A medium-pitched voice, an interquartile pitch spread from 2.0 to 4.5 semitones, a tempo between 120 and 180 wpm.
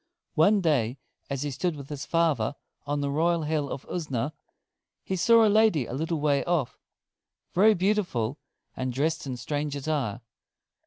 Yes: medium, 150 Hz; average, 3.8 semitones; average, 160 wpm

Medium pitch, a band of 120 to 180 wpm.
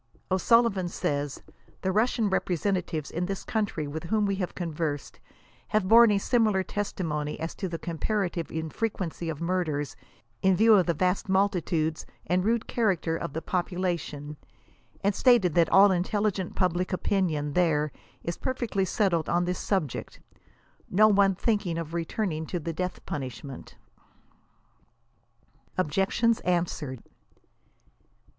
Yes: medium, 180 Hz; slow, 135 wpm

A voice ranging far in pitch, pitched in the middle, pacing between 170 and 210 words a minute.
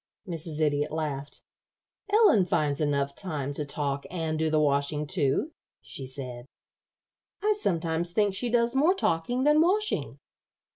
No: wide, 7.4 semitones; medium, 160 Hz; average, 140 wpm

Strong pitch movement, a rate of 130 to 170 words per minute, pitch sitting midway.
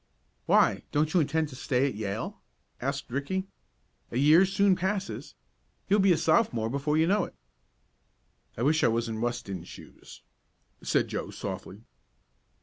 Yes: wide, 7.1 semitones; average, 150 wpm; medium, 145 Hz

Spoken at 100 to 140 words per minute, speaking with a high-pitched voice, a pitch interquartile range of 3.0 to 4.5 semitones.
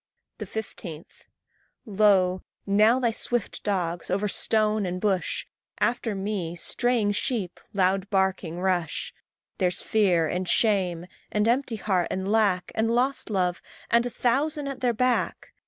Yes: slow, 135 wpm; high, 205 Hz; average, 3.8 semitones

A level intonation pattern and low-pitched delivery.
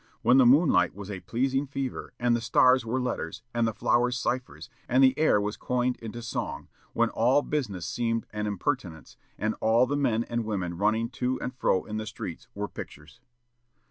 No: average, 3.3 semitones; low, 120 Hz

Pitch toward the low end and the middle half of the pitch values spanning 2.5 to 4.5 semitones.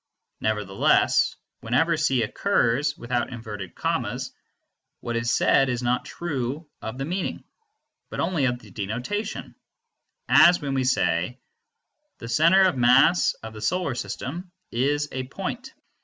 No: low, 130 Hz; wide, 5.6 semitones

